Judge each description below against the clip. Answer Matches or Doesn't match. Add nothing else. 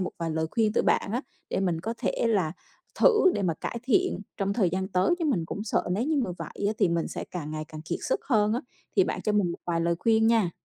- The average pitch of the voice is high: Matches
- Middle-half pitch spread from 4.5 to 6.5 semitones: Matches